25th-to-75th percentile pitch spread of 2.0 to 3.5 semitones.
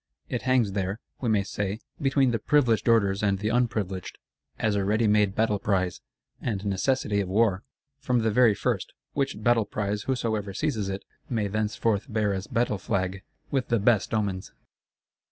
Yes: average, 2.9 semitones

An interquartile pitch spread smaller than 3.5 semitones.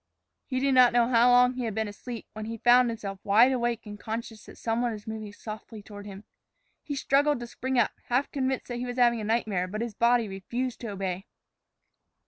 Yes: narrow, 2.6 semitones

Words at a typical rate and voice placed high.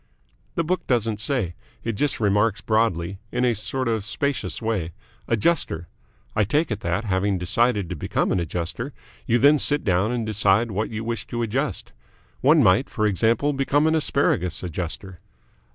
No: average, 170 wpm; low, 110 Hz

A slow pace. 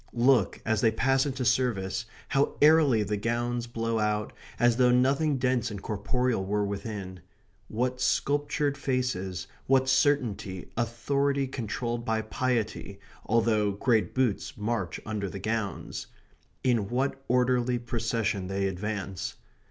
Yes: slow, 130 wpm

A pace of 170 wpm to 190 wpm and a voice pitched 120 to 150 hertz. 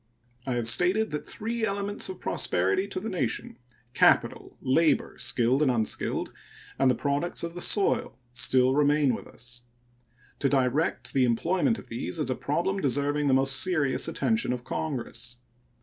No: average, 155 wpm; medium, 140 Hz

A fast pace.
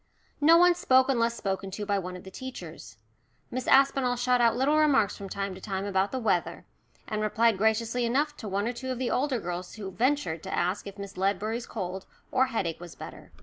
Yes: fast, 215 wpm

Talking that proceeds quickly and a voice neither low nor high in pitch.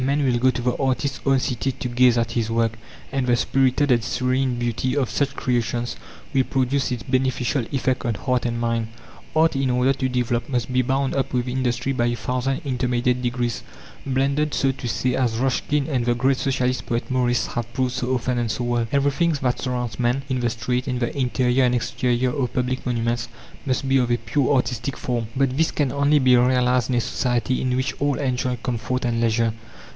No: fast, 210 wpm; low, 125 Hz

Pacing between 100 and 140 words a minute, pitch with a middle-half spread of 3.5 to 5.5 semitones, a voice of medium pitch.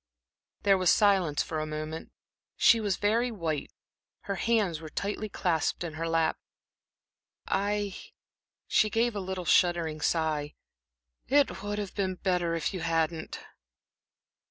Yes: slow, 135 wpm; average, 4.1 semitones; medium, 180 Hz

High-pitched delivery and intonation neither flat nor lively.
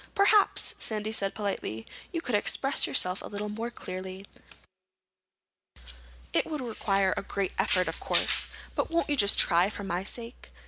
Yes: high, 205 Hz; average, 4.0 semitones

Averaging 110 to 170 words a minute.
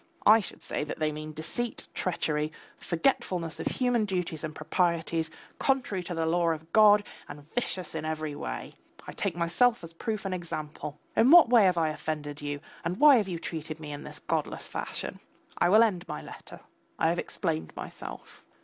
No: average, 190 wpm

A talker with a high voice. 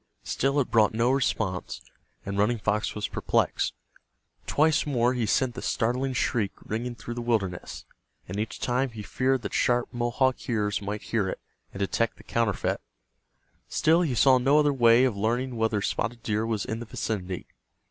No: low, 115 Hz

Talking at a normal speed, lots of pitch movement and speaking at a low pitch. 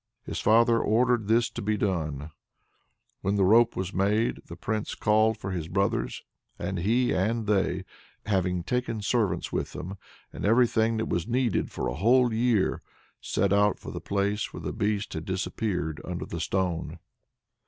No: average, 165 wpm; average, 3.4 semitones; low, 105 Hz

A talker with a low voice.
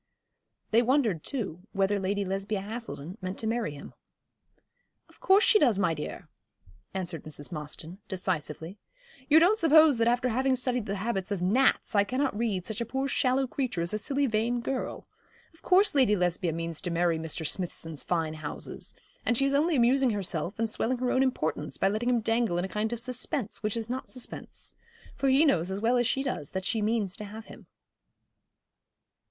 No: high, 215 Hz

